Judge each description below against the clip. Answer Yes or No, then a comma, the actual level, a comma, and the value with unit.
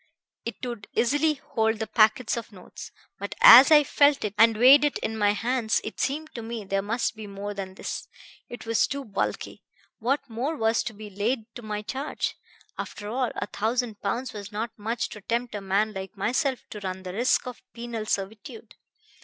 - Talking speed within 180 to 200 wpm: Yes, average, 195 wpm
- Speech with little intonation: No, average, 3.3 semitones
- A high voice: Yes, high, 225 Hz